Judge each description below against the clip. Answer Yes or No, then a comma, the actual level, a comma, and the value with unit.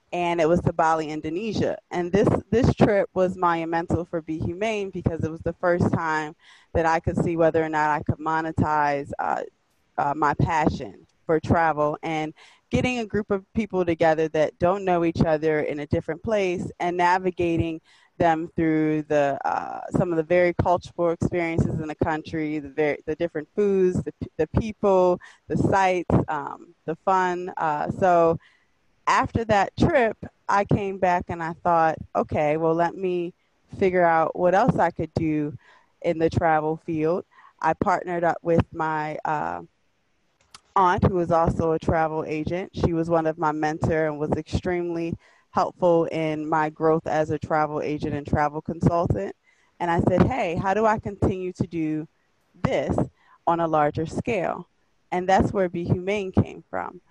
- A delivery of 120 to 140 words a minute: No, average, 170 wpm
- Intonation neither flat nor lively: No, narrow, 2.3 semitones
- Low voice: No, medium, 165 Hz